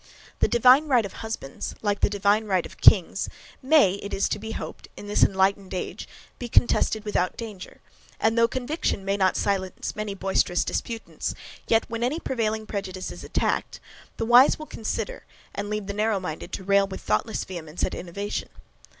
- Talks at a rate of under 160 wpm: No, average, 180 wpm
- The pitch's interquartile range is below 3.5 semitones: Yes, average, 3.0 semitones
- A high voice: Yes, high, 205 Hz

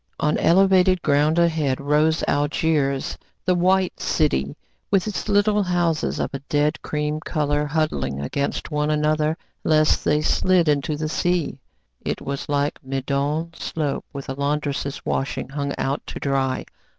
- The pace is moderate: Yes, average, 145 wpm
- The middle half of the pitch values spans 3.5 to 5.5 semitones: No, average, 2.7 semitones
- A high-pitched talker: No, medium, 150 Hz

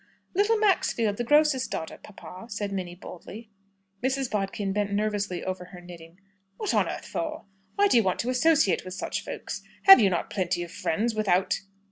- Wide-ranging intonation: Yes, wide, 5.8 semitones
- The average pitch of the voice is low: No, high, 205 Hz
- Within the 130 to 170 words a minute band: No, average, 180 wpm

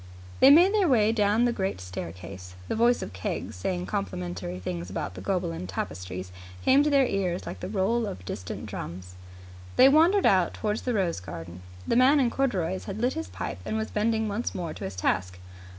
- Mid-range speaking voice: Yes, medium, 180 Hz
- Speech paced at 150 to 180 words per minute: No, average, 200 wpm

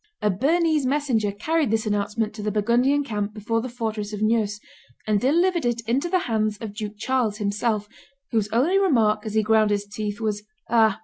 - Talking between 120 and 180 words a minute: No, average, 190 wpm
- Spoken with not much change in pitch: No, average, 3.4 semitones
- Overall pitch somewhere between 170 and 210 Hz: No, high, 220 Hz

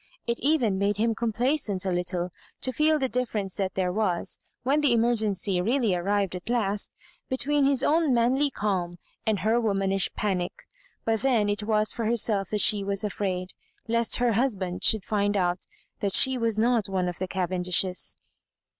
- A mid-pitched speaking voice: No, high, 210 Hz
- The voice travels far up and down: No, average, 3.9 semitones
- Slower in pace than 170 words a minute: No, average, 180 wpm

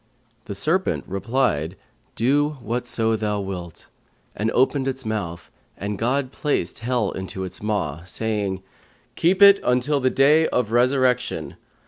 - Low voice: Yes, low, 115 Hz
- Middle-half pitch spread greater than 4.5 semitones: Yes, average, 5.2 semitones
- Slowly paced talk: Yes, slow, 130 wpm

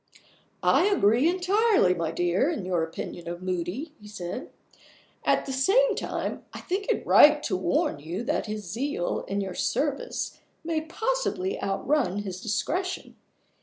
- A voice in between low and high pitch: No, high, 230 Hz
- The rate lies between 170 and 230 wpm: No, average, 150 wpm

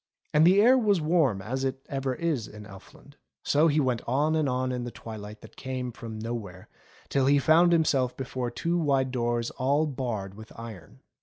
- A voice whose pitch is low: Yes, low, 130 Hz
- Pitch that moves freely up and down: No, average, 4.5 semitones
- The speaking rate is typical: Yes, average, 190 wpm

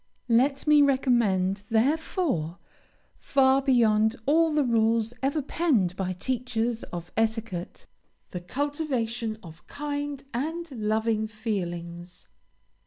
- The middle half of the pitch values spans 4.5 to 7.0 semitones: Yes, average, 5.1 semitones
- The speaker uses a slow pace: Yes, slow, 105 wpm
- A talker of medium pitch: No, high, 230 Hz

